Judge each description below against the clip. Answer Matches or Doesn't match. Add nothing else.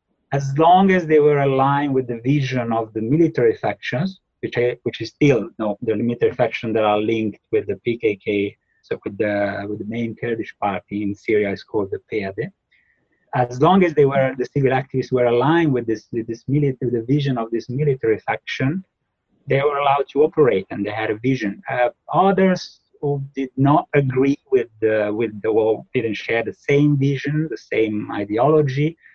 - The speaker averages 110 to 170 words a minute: Doesn't match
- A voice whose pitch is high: Doesn't match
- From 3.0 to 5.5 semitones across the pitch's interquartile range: Matches